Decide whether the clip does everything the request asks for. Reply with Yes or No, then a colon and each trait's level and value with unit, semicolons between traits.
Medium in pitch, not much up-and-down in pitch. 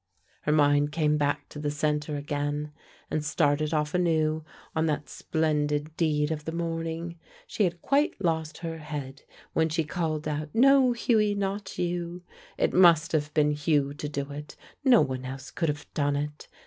Yes: medium, 155 Hz; narrow, 2.2 semitones